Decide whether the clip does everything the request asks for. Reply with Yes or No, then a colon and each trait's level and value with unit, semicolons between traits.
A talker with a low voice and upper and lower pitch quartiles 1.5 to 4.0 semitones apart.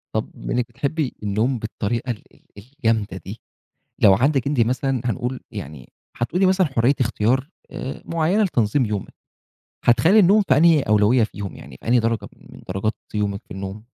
No: low, 120 Hz; average, 4.9 semitones